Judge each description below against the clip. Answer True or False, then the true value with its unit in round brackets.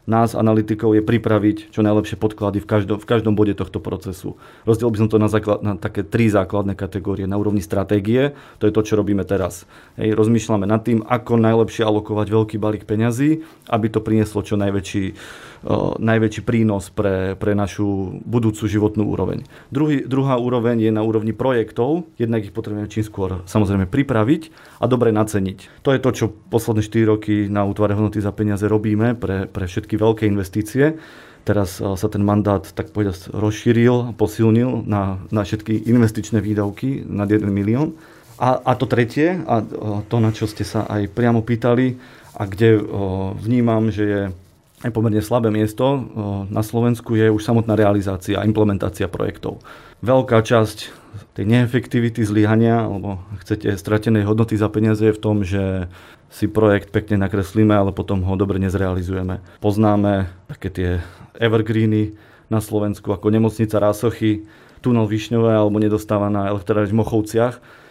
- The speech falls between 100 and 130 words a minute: False (160 wpm)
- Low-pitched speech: True (110 Hz)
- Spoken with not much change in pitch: True (2.0 semitones)